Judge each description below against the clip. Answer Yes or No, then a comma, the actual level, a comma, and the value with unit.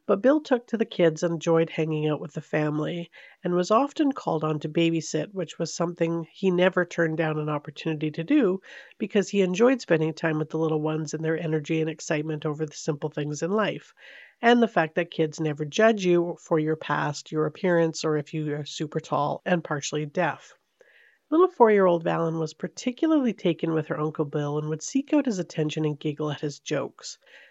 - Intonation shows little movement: No, average, 3.1 semitones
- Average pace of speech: No, fast, 210 wpm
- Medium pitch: Yes, medium, 165 Hz